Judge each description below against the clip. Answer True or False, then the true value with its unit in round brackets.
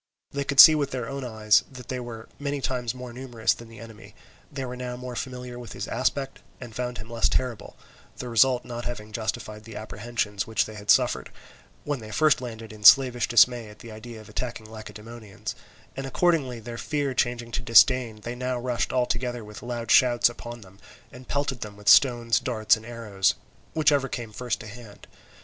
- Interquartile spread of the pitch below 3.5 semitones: True (2.4 semitones)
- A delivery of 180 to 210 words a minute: True (200 wpm)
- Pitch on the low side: True (120 Hz)